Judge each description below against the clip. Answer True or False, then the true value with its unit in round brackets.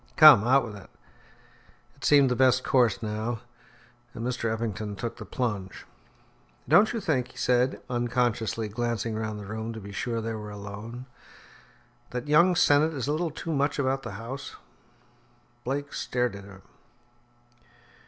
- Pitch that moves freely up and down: False (3.8 semitones)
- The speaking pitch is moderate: False (120 Hz)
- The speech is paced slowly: False (155 wpm)